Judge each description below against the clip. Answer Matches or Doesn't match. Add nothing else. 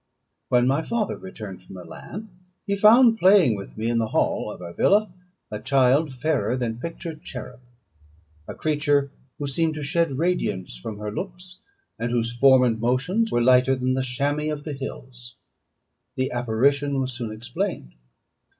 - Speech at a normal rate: Matches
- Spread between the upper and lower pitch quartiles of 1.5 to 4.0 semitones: Doesn't match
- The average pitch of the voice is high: Doesn't match